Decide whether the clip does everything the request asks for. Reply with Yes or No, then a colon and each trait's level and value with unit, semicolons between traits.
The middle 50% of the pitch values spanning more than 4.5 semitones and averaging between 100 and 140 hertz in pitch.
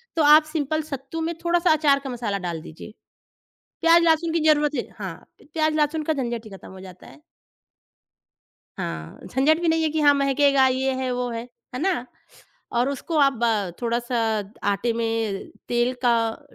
No: average, 5.1 semitones; very high, 270 Hz